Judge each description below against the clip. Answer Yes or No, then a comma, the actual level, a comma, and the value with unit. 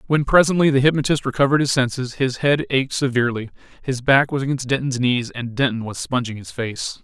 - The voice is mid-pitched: No, low, 130 Hz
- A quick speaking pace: No, average, 195 wpm